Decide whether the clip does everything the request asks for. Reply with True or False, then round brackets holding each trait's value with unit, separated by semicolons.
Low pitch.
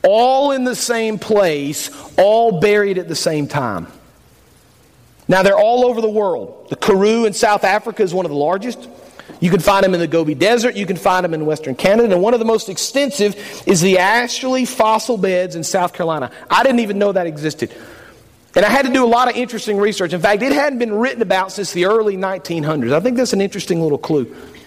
False (200 Hz)